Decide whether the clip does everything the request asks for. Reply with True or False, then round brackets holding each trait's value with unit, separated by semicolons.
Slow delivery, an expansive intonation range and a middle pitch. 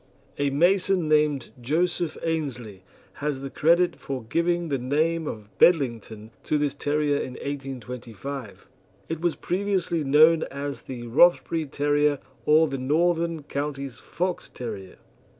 False (130 wpm; 3.9 semitones; 145 Hz)